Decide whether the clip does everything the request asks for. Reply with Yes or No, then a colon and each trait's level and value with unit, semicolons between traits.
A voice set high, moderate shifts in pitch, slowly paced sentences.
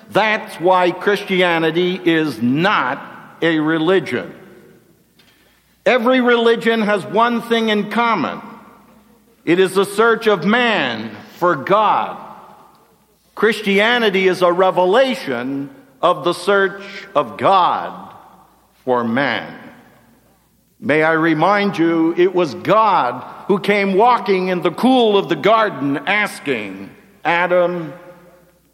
Yes: high, 195 Hz; average, 4.3 semitones; slow, 105 wpm